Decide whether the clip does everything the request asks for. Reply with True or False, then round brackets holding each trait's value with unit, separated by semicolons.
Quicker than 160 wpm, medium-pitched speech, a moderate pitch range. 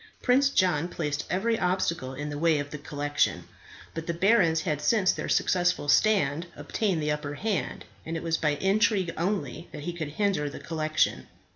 True (180 wpm; 165 Hz; 4.2 semitones)